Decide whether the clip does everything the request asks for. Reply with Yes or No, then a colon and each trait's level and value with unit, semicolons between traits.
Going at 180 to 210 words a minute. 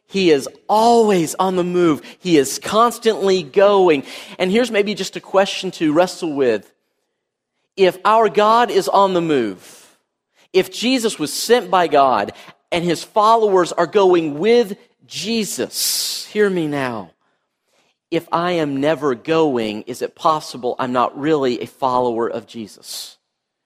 No: average, 145 wpm